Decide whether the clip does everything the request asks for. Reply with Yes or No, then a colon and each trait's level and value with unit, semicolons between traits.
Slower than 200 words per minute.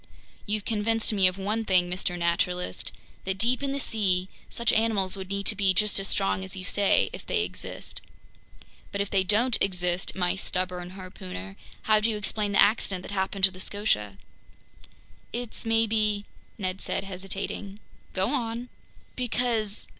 Yes: average, 165 wpm